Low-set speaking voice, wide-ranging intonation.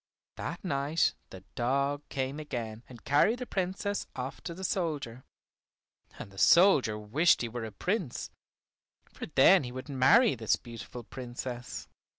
Yes: low, 130 Hz; wide, 5.8 semitones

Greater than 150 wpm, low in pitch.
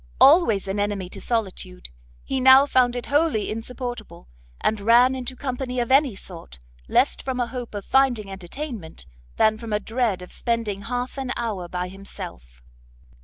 No: average, 165 wpm; high, 230 Hz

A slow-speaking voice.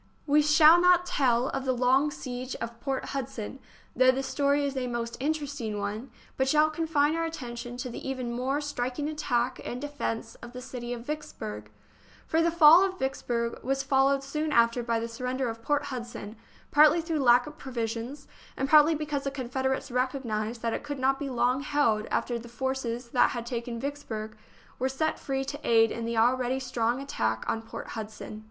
No: average, 195 wpm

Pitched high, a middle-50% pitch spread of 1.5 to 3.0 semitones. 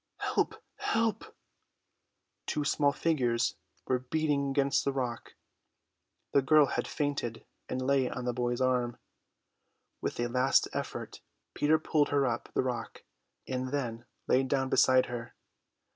No: low, 130 Hz; narrow, 2.6 semitones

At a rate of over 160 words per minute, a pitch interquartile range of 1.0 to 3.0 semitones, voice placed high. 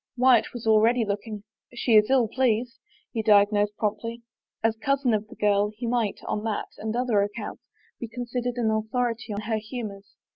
Yes: average, 180 wpm; narrow, 2.4 semitones; high, 225 Hz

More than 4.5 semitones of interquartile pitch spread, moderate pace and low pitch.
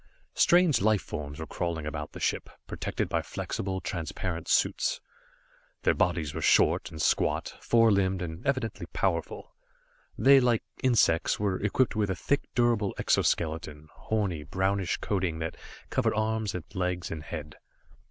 Yes: average, 5.2 semitones; average, 145 wpm; very low, 95 Hz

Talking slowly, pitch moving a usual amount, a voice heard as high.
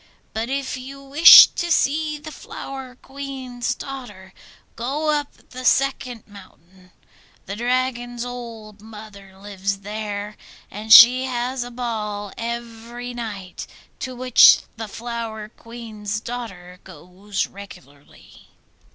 Yes: slow, 115 wpm; average, 3.7 semitones; high, 235 Hz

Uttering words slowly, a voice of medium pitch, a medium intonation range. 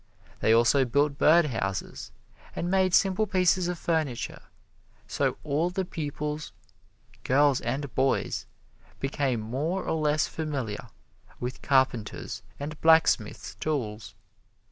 Yes: slow, 115 wpm; medium, 145 Hz; average, 4.1 semitones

